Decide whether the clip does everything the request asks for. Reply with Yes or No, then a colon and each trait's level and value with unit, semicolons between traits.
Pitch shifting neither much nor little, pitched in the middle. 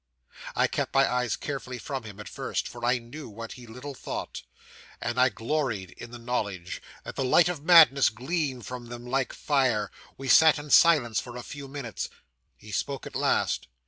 No: average, 3.2 semitones; low, 125 Hz